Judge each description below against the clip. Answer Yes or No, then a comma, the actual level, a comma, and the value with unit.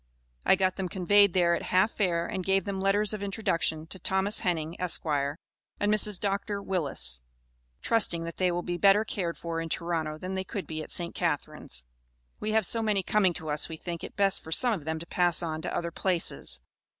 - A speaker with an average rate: No, fast, 210 wpm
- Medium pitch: Yes, medium, 180 Hz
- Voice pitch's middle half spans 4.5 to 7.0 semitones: No, average, 3.2 semitones